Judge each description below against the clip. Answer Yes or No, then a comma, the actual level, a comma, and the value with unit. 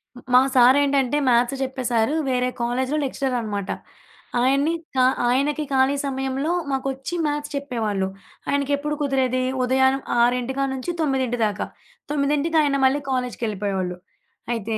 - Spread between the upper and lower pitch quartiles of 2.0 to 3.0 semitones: Yes, narrow, 2.5 semitones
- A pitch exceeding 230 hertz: Yes, very high, 265 Hz